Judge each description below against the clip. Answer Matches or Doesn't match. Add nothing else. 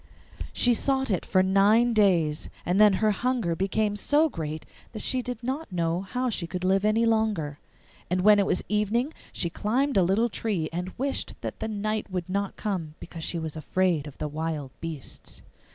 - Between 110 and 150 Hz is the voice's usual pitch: Doesn't match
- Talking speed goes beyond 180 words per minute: Matches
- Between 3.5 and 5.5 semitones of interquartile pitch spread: Matches